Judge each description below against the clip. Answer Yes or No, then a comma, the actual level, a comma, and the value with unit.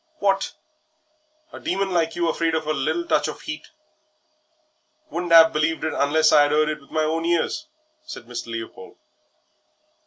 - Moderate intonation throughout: No, narrow, 2.0 semitones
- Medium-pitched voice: Yes, medium, 160 Hz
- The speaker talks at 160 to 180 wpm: Yes, average, 165 wpm